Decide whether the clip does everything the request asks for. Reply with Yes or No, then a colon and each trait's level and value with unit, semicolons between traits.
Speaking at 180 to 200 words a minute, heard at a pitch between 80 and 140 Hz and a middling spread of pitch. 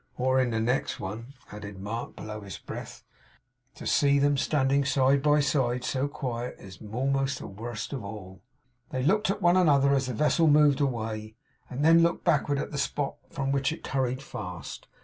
Yes: average, 190 wpm; low, 135 Hz; average, 3.9 semitones